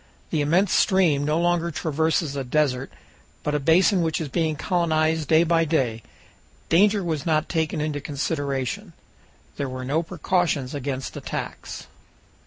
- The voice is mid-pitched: Yes, medium, 155 Hz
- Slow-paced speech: No, average, 145 wpm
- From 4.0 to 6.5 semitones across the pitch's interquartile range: No, average, 2.9 semitones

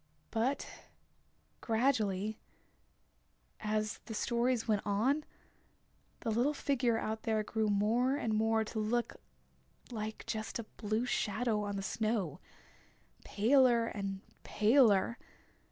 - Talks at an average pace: No, slow, 110 wpm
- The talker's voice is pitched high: Yes, high, 220 Hz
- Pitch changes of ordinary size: No, narrow, 2.2 semitones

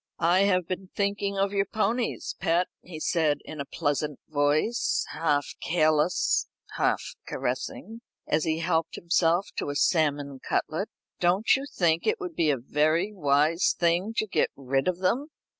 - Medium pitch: Yes, medium, 170 Hz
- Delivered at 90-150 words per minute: No, average, 160 wpm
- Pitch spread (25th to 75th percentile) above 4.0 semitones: Yes, average, 4.6 semitones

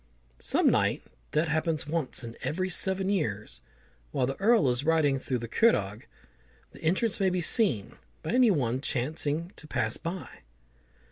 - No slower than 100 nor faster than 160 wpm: Yes, average, 155 wpm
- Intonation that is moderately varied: No, wide, 6.7 semitones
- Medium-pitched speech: Yes, medium, 155 Hz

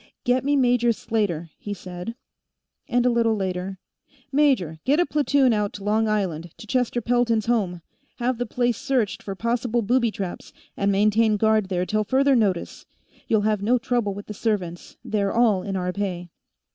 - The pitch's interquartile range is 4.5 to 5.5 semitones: No, average, 3.8 semitones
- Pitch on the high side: Yes, high, 215 Hz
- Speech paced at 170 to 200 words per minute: Yes, average, 175 wpm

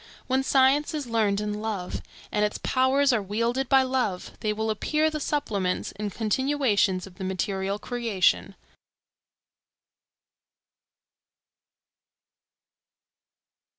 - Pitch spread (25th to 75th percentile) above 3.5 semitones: Yes, average, 4.7 semitones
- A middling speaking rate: No, slow, 105 wpm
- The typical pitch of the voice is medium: No, high, 220 Hz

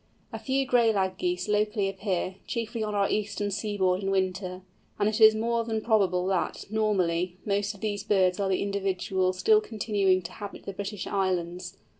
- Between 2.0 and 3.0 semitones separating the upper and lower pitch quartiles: Yes, narrow, 2.4 semitones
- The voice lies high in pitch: Yes, high, 200 Hz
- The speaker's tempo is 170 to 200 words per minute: Yes, average, 180 wpm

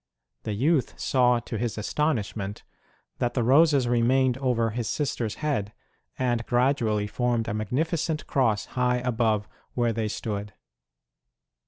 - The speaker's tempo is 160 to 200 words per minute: No, slow, 135 wpm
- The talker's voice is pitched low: Yes, low, 120 Hz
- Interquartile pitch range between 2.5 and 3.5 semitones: Yes, average, 3.2 semitones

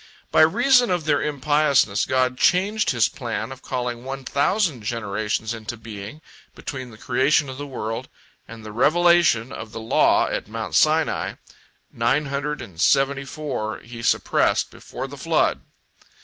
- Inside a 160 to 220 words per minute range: No, average, 150 wpm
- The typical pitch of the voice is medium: No, low, 130 Hz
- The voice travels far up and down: No, average, 4.9 semitones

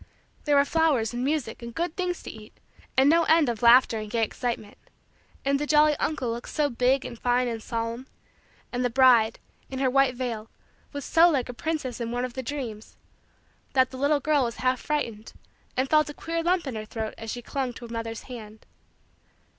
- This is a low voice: No, very high, 255 Hz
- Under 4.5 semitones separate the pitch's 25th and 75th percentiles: Yes, average, 3.9 semitones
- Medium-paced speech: No, fast, 210 wpm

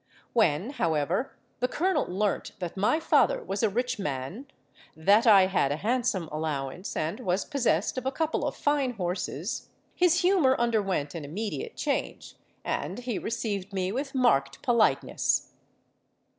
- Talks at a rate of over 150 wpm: No, average, 145 wpm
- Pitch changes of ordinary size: No, wide, 6.5 semitones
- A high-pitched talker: Yes, high, 210 Hz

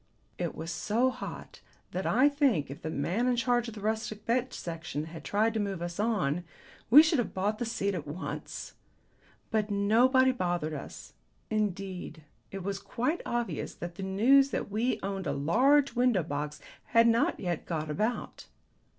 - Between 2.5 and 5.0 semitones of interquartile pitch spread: No, wide, 5.6 semitones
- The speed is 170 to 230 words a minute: Yes, average, 175 wpm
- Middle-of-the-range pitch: No, high, 205 Hz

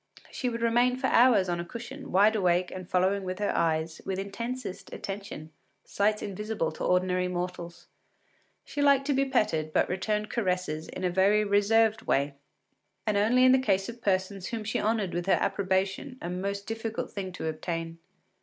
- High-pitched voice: Yes, high, 200 Hz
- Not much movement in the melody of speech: No, average, 3.7 semitones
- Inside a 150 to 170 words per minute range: No, average, 180 wpm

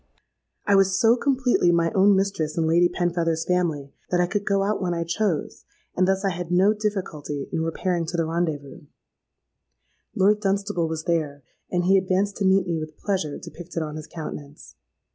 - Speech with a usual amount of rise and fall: Yes, average, 3.2 semitones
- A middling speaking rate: Yes, average, 185 wpm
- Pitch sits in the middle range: Yes, medium, 175 Hz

